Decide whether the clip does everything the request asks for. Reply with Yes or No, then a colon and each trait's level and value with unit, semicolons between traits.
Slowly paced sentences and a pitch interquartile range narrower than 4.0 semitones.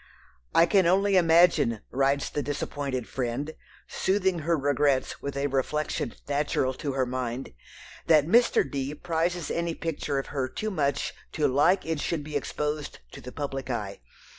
No: average, 160 wpm; average, 3.6 semitones